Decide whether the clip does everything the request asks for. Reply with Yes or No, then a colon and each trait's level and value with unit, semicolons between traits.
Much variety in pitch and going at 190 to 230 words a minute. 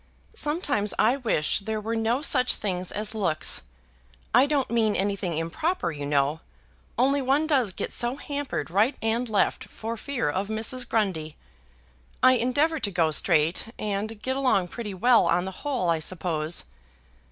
No: wide, 6.2 semitones; average, 160 wpm